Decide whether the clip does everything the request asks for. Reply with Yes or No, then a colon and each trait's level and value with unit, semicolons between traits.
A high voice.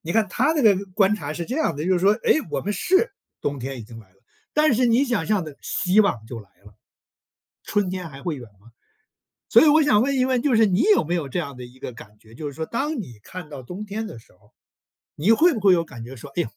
No: medium, 180 Hz